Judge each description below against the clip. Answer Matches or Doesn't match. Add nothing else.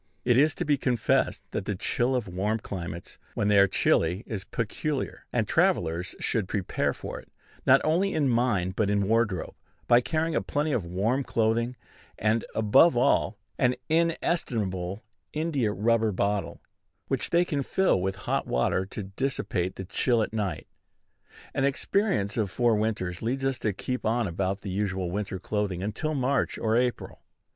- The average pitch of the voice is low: Matches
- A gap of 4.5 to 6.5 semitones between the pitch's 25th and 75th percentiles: Matches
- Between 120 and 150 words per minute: Doesn't match